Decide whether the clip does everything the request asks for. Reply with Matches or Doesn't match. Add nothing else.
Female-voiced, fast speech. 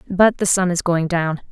Matches